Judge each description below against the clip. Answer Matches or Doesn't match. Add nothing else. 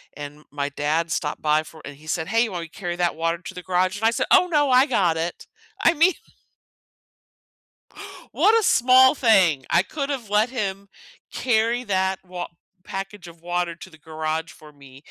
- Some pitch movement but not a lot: Doesn't match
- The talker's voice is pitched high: Doesn't match